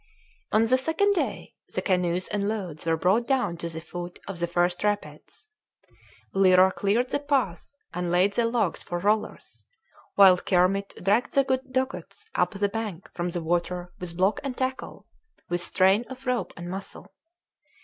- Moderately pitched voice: No, high, 195 Hz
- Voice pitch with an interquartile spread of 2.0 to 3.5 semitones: No, average, 4.8 semitones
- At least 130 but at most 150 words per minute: No, average, 165 wpm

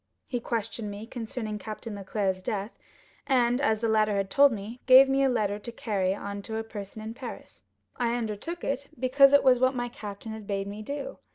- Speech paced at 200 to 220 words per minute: Yes, fast, 205 wpm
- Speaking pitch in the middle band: No, high, 225 Hz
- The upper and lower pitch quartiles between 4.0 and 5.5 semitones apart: No, average, 3.6 semitones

